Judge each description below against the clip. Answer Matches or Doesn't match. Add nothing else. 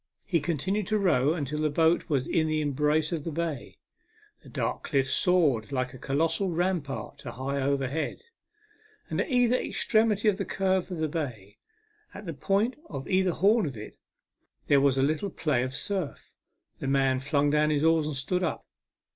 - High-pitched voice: Doesn't match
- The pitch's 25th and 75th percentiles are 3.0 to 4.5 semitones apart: Doesn't match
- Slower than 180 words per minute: Doesn't match